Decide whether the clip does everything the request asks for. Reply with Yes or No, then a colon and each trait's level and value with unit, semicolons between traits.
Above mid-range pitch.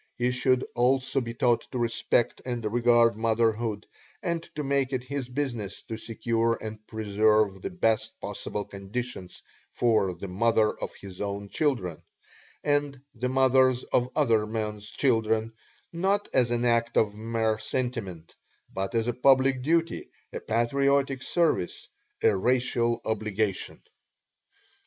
No: low, 115 Hz